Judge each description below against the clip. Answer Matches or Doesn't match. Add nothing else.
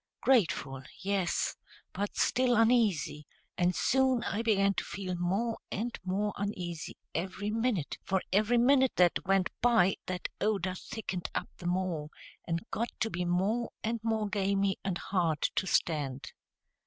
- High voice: Matches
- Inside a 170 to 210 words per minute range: Doesn't match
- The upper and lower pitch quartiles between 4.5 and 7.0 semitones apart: Doesn't match